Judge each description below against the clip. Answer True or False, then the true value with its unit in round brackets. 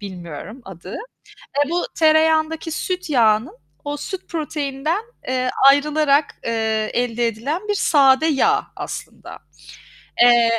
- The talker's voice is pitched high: True (280 Hz)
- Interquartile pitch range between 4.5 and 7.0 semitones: True (5.4 semitones)